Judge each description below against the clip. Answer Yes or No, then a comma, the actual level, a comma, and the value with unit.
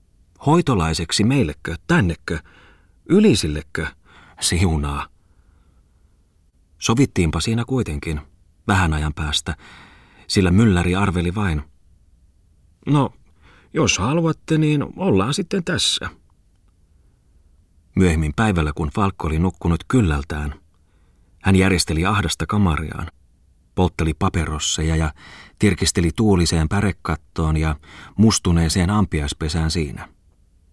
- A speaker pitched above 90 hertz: No, very low, 85 Hz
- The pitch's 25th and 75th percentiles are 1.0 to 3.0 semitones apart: No, average, 3.6 semitones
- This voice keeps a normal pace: No, slow, 85 wpm